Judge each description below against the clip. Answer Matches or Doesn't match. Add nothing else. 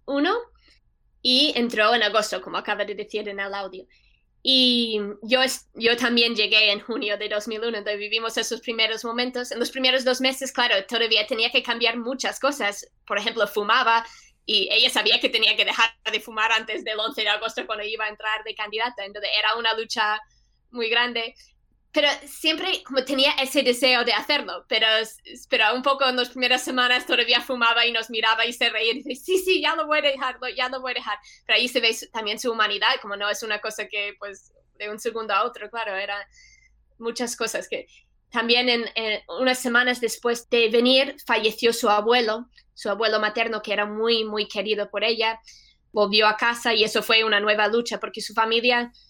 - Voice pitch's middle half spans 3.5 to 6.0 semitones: Doesn't match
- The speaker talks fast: Matches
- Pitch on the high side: Matches